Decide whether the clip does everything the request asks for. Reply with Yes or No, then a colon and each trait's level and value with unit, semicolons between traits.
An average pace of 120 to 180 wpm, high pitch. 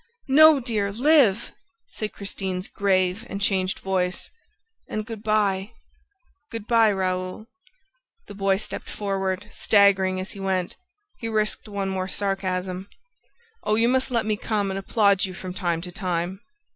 Yes: average, 150 wpm; high, 195 Hz